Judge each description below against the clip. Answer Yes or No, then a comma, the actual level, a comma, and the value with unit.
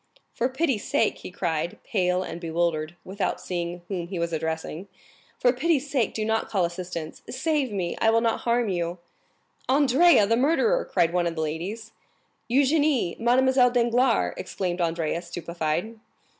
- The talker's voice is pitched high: Yes, high, 195 Hz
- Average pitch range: No, wide, 6.4 semitones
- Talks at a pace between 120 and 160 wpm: Yes, average, 145 wpm